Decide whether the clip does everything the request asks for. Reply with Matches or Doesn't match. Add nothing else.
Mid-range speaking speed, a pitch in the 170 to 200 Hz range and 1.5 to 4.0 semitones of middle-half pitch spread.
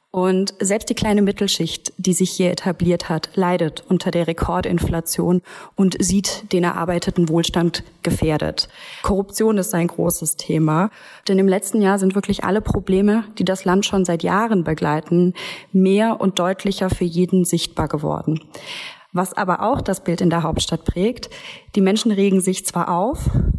Matches